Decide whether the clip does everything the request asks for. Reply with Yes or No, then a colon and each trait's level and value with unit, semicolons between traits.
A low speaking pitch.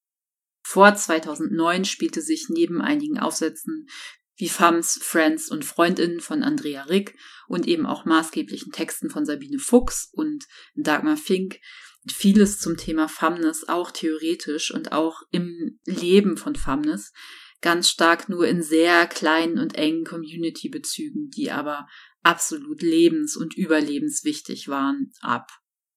No: high, 190 Hz